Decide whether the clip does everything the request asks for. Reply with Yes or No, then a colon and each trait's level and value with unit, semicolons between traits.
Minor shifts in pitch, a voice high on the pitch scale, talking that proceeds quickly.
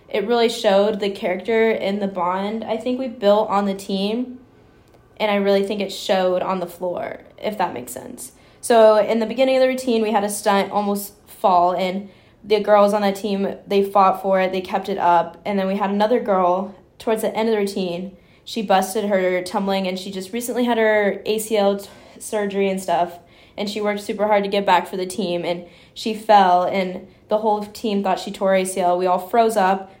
Yes: narrow, 2.2 semitones; high, 200 Hz; fast, 215 wpm